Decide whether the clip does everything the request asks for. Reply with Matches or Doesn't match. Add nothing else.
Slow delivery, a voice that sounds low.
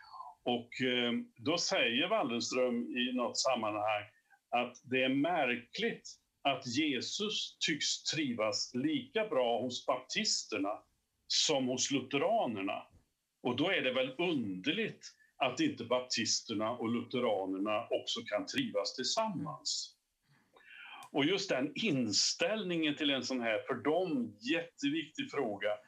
Doesn't match